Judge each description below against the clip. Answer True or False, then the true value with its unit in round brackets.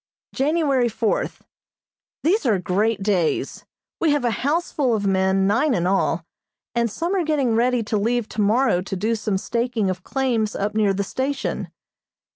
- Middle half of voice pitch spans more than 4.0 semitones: True (5.1 semitones)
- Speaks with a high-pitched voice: True (225 Hz)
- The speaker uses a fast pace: False (160 wpm)